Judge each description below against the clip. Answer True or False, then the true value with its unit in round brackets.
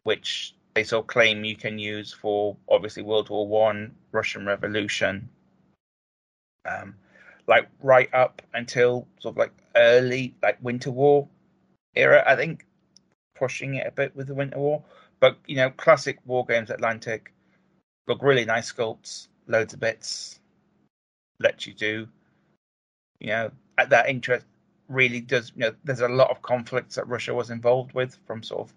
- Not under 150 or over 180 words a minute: True (160 wpm)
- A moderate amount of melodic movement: True (3.0 semitones)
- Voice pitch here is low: True (125 Hz)